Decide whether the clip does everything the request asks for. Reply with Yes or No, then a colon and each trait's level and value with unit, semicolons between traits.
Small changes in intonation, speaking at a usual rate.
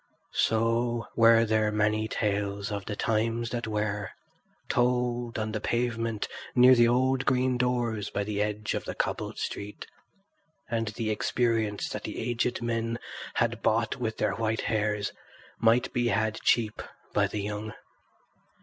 Yes: narrow, 1.9 semitones; average, 150 wpm